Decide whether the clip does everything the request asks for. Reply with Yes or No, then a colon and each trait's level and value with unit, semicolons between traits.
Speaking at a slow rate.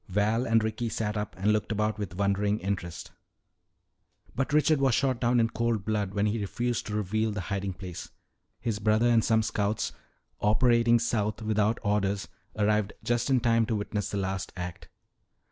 No: average, 175 wpm